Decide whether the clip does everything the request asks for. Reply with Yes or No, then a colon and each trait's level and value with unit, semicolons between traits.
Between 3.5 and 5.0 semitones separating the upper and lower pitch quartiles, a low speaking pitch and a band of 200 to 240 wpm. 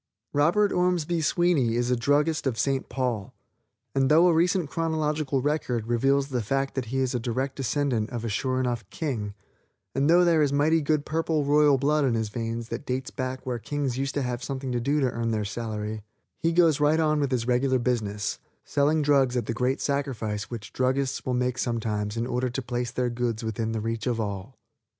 Yes: average, 3.8 semitones; low, 130 Hz; fast, 205 wpm